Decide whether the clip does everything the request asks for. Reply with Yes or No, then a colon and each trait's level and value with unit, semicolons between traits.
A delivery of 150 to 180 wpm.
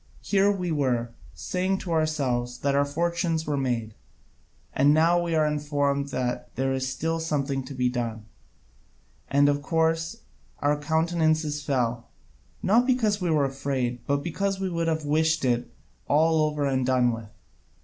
Yes: average, 155 wpm